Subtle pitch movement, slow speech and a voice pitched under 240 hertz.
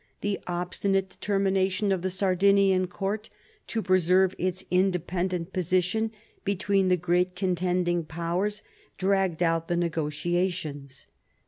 Yes: narrow, 1.8 semitones; slow, 110 wpm; medium, 185 Hz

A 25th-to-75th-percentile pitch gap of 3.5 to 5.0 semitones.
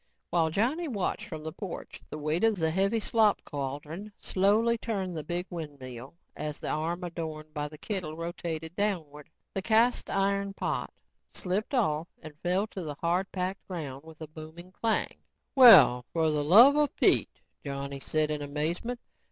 Yes: average, 4.5 semitones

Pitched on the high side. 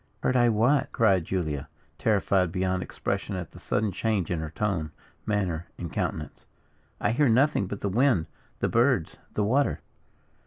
No: low, 100 Hz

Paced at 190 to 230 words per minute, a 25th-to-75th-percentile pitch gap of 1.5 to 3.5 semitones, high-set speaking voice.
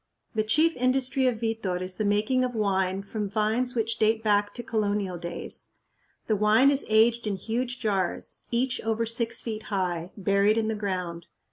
No: average, 175 wpm; average, 2.8 semitones; high, 215 Hz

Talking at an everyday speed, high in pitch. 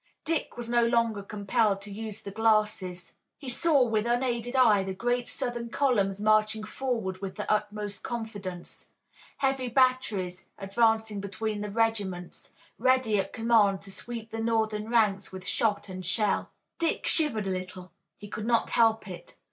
Yes: average, 155 wpm; high, 220 Hz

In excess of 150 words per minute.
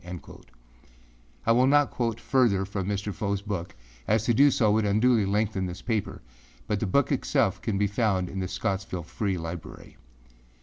Yes: average, 175 wpm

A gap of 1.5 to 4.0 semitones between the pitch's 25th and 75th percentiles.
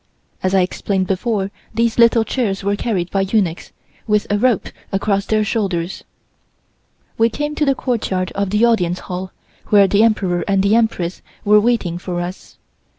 Yes: average, 3.3 semitones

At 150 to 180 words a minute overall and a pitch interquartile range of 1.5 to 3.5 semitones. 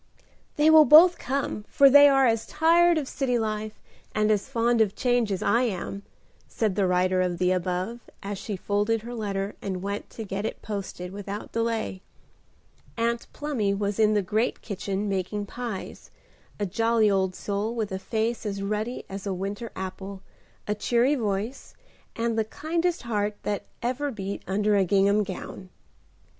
Yes: average, 170 wpm; average, 3.1 semitones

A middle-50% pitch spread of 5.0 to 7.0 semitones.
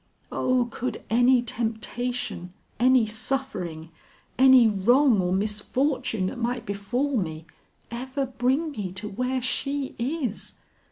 No: average, 3.9 semitones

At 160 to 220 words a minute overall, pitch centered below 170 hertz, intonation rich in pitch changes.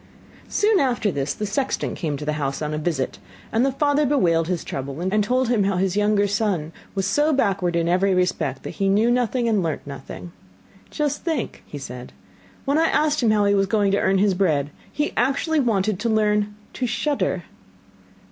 No: average, 200 wpm; high, 200 Hz; wide, 6.7 semitones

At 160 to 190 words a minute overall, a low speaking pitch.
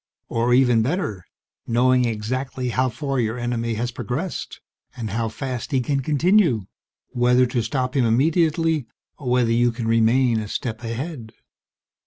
No: average, 150 wpm; low, 125 Hz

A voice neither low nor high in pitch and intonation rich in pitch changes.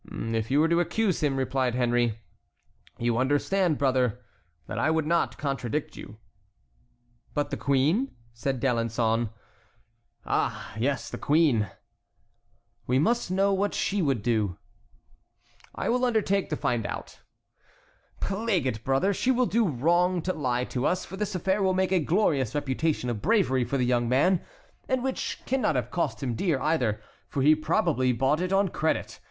Yes: medium, 145 Hz; wide, 6.9 semitones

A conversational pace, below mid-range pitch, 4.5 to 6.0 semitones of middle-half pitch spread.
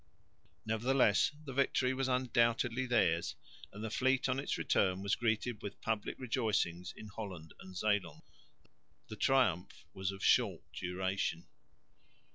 No: slow, 130 wpm; low, 110 Hz; average, 5.0 semitones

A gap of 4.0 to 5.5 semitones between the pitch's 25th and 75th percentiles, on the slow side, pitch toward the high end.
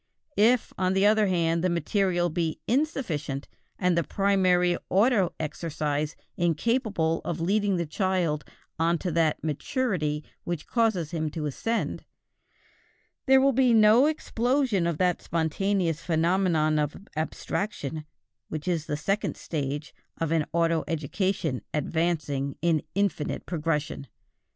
No: average, 4.3 semitones; slow, 125 wpm; medium, 170 Hz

